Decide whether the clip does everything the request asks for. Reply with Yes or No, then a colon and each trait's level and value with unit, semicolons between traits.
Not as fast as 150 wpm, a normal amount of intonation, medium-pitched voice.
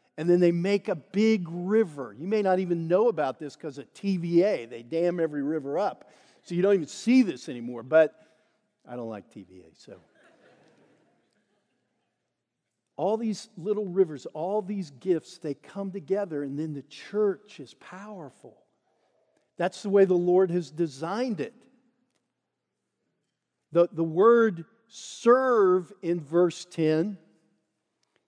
Yes: average, 140 wpm; average, 4.5 semitones; medium, 180 Hz